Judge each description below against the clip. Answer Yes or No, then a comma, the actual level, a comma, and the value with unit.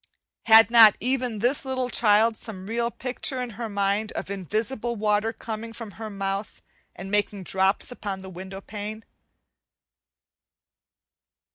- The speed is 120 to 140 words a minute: Yes, slow, 135 wpm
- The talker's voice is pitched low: No, high, 215 Hz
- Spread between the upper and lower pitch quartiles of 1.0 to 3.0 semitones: Yes, average, 2.7 semitones